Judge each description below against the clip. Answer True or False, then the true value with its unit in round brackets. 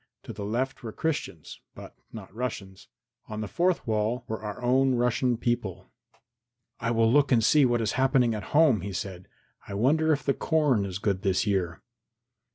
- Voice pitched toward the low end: True (115 Hz)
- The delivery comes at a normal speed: True (180 wpm)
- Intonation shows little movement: False (4.6 semitones)